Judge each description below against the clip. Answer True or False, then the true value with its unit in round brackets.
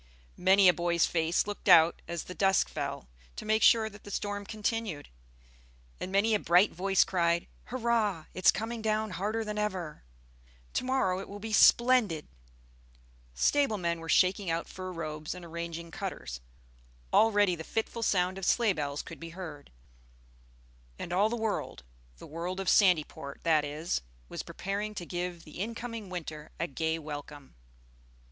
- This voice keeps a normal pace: True (165 wpm)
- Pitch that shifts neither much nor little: True (4.2 semitones)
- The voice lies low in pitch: False (185 Hz)